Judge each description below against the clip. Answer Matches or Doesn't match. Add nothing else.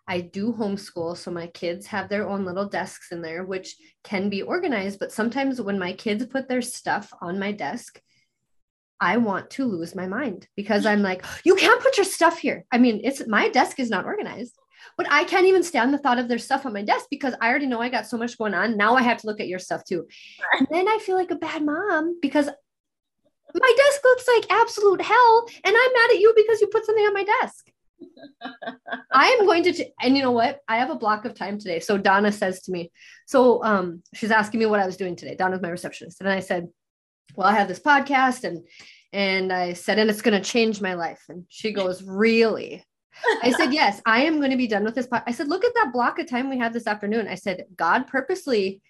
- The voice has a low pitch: Doesn't match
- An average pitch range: Doesn't match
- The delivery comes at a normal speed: Doesn't match